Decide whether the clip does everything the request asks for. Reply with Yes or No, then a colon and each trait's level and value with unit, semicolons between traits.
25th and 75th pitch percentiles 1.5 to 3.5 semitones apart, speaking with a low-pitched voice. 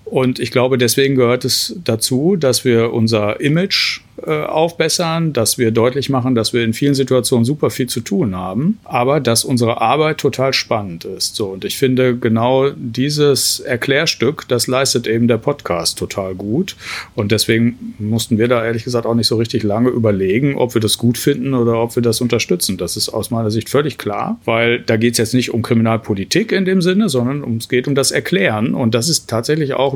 Yes: average, 2.9 semitones; low, 120 Hz